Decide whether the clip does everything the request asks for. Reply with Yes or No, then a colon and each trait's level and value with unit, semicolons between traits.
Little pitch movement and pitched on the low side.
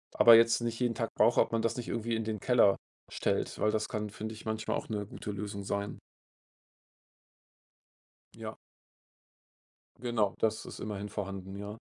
Yes: narrow, 1.9 semitones; low, 110 Hz